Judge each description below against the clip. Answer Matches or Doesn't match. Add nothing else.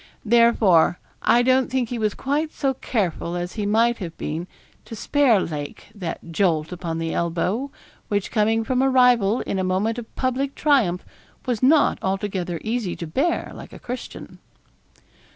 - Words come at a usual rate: Matches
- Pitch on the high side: Matches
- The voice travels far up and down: Matches